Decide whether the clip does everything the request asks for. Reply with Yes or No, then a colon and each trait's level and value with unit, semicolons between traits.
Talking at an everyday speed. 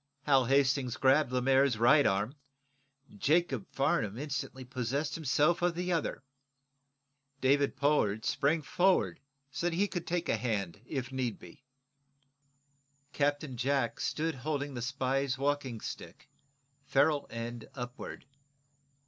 No: slow, 125 wpm